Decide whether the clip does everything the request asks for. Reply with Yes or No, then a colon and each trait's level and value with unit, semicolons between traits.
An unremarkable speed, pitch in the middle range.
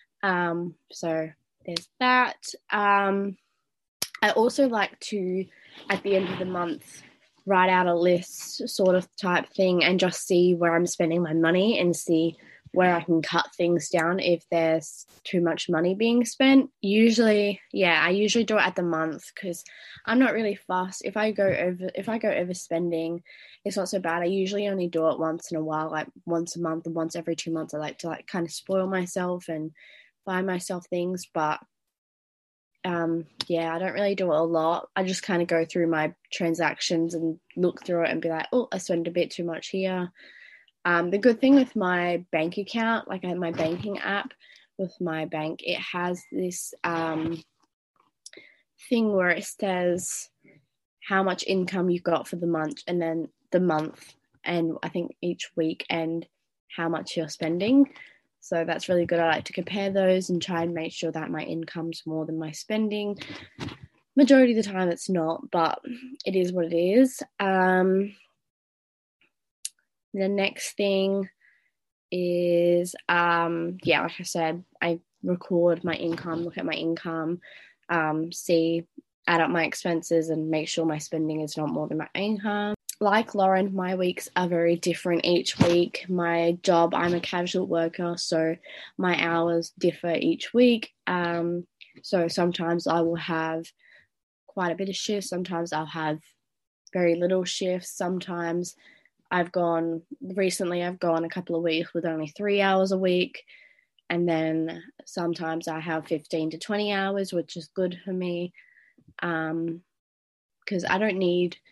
Yes: average, 175 wpm; medium, 175 Hz